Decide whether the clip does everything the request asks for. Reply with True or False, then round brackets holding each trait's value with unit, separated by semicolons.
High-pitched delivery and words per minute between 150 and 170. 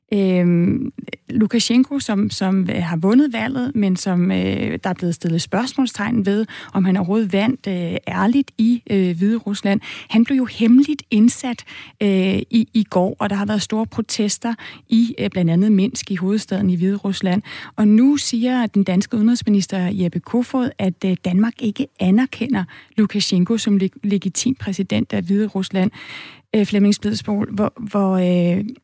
True (205 Hz; 160 wpm)